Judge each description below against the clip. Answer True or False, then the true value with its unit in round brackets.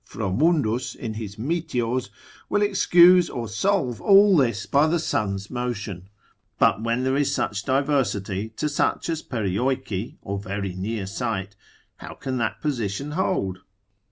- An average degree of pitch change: False (6.5 semitones)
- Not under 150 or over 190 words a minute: False (140 wpm)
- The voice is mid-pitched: False (120 Hz)